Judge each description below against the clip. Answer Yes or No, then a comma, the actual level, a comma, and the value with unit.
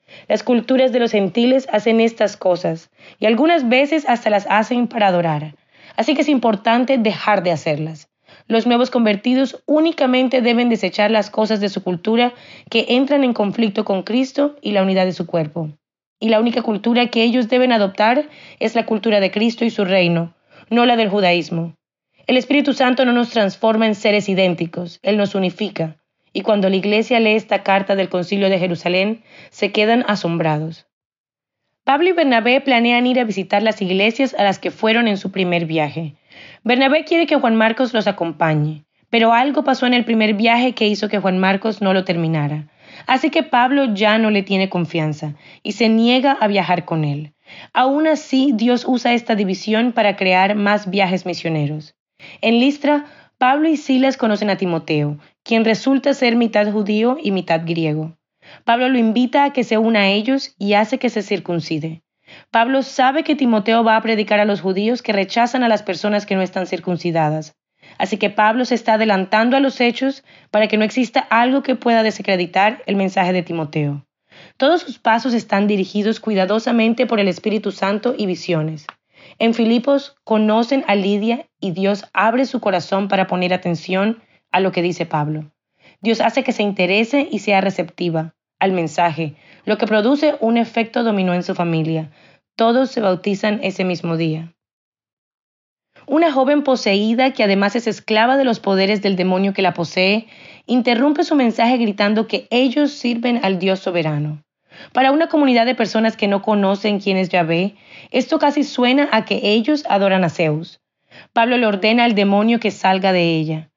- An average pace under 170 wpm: No, average, 175 wpm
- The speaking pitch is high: Yes, high, 215 Hz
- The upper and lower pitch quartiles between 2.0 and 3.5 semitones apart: No, average, 4.6 semitones